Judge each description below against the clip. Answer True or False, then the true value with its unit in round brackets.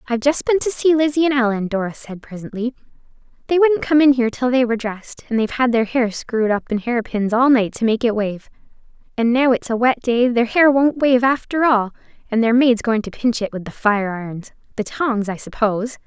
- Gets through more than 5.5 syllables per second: True (5.8 syllables/s)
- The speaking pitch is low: False (240 Hz)